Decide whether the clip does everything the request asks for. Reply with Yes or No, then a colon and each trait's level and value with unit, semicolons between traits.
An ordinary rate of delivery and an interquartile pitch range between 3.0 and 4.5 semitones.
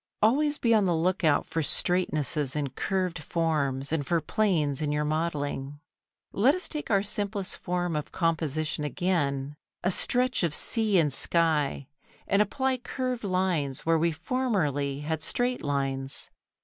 No: average, 150 wpm; wide, 5.4 semitones